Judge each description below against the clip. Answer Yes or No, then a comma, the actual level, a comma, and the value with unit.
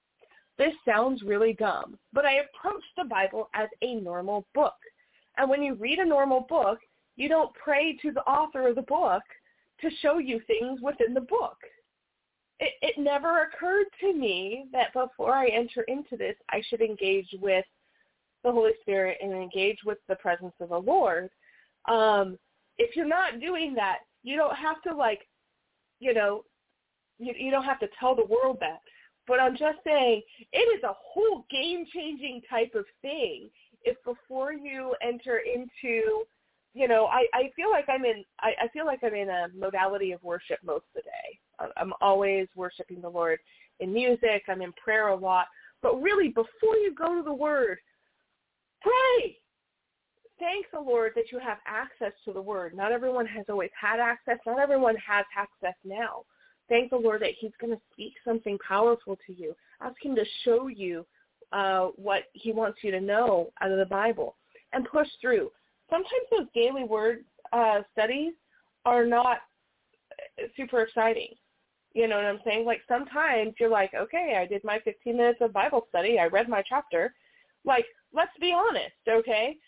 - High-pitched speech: Yes, high, 240 Hz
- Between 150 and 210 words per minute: Yes, average, 175 wpm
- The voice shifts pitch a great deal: Yes, wide, 6.2 semitones